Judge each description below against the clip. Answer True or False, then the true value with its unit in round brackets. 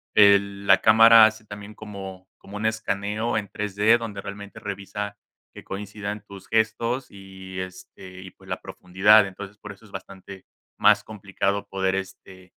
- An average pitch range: False (1.7 semitones)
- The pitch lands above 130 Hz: False (100 Hz)